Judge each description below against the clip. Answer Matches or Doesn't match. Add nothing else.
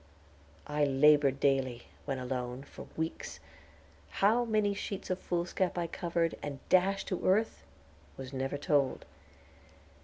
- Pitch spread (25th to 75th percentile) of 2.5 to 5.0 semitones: Doesn't match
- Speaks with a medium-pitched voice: Matches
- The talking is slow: Matches